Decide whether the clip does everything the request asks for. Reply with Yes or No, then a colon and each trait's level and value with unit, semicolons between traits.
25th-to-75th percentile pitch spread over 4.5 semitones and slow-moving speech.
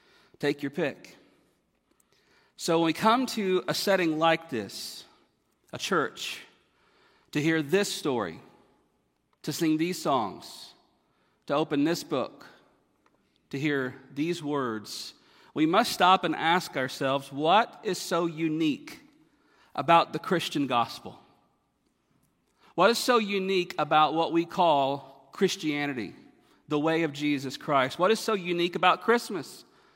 Yes: average, 5.0 semitones; slow, 130 wpm